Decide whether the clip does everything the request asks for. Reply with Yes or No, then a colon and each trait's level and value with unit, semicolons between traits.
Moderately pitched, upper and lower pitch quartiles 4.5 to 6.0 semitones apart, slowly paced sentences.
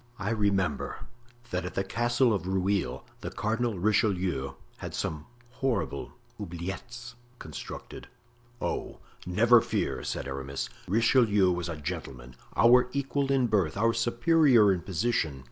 No: low, 105 Hz; average, 5.2 semitones; slow, 130 wpm